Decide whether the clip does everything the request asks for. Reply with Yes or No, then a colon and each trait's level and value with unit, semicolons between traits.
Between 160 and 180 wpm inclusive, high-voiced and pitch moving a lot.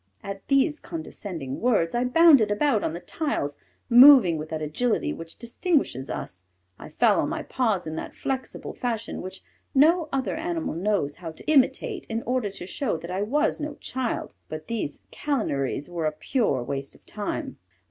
Yes: average, 175 wpm; high, 220 Hz; wide, 9.0 semitones